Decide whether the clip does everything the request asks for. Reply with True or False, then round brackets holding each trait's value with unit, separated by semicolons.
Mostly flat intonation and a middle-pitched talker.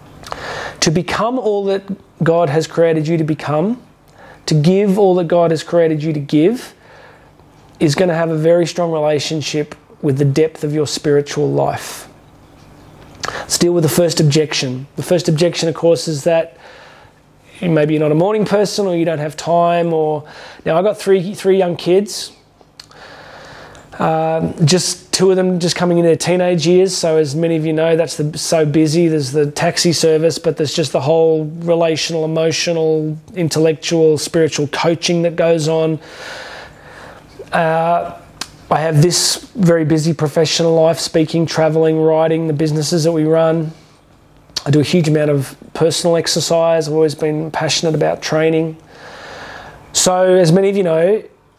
True (1.7 semitones; 165 Hz)